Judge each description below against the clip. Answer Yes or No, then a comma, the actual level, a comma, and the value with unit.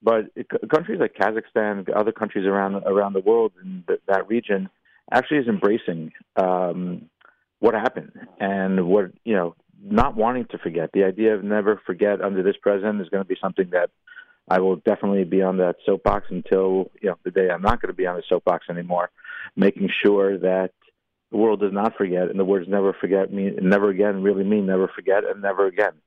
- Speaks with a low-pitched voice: Yes, low, 100 Hz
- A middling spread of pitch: No, narrow, 1.9 semitones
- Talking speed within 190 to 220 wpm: Yes, average, 200 wpm